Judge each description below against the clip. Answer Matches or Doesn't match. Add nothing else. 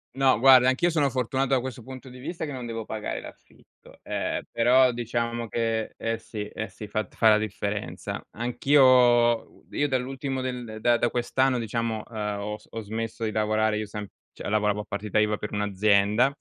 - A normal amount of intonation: Matches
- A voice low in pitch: Matches